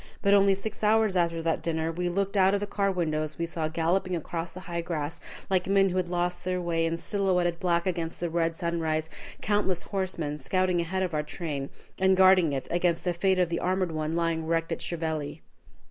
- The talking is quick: Yes, fast, 215 wpm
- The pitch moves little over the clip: Yes, narrow, 2.3 semitones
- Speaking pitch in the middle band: Yes, medium, 175 Hz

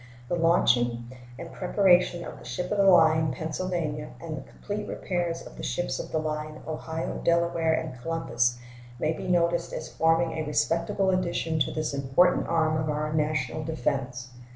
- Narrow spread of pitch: Yes, narrow, 2.3 semitones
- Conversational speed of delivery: Yes, average, 170 wpm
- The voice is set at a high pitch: No, medium, 160 Hz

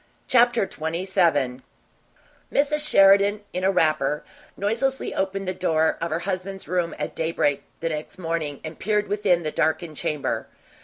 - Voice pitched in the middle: Yes, medium, 180 Hz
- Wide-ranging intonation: No, average, 3.9 semitones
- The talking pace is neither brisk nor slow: Yes, average, 145 wpm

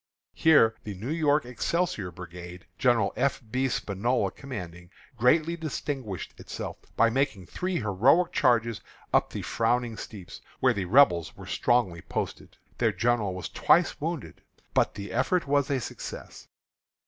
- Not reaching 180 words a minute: Yes, average, 140 wpm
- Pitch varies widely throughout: Yes, wide, 6.1 semitones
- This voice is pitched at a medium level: No, low, 120 Hz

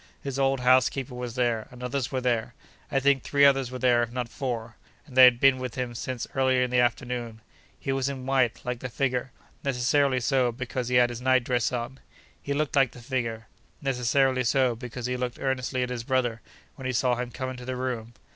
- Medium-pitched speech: No, low, 125 Hz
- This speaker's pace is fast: Yes, fast, 210 wpm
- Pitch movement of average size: No, narrow, 1.5 semitones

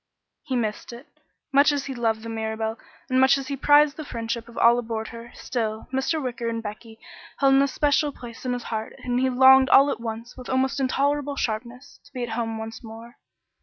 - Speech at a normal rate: No, fast, 210 wpm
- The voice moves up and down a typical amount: Yes, average, 3.0 semitones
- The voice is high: Yes, high, 245 Hz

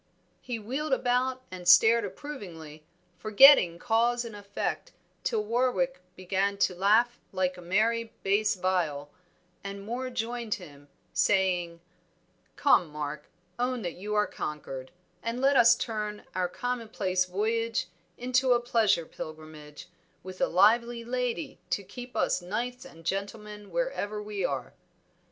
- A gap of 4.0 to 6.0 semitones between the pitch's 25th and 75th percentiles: Yes, average, 4.8 semitones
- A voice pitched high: Yes, high, 210 Hz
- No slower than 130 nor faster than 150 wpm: Yes, slow, 135 wpm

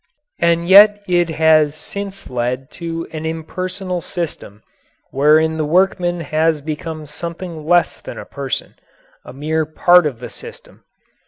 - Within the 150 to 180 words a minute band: No, average, 140 wpm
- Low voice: No, medium, 160 Hz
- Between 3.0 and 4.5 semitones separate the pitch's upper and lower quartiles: No, narrow, 2.5 semitones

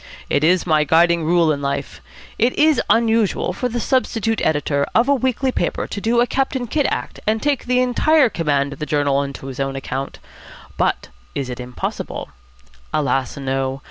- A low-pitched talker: No, medium, 170 Hz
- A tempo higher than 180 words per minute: No, average, 175 wpm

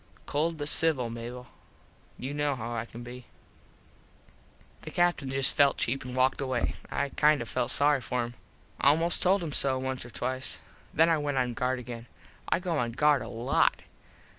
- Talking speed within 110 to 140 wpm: No, average, 185 wpm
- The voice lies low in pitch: Yes, low, 130 Hz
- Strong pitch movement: No, average, 3.2 semitones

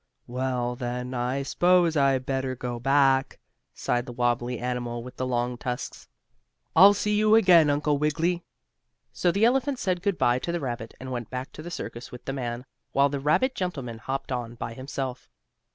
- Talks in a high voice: No, low, 130 Hz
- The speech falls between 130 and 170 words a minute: No, average, 185 wpm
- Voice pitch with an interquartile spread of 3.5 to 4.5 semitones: No, average, 5.1 semitones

